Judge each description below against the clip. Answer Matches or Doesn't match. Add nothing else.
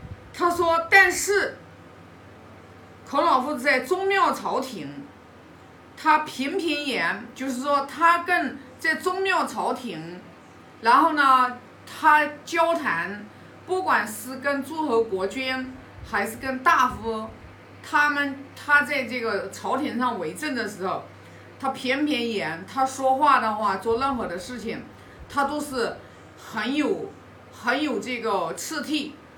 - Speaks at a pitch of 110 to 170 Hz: Doesn't match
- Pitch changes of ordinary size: Matches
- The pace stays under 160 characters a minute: Doesn't match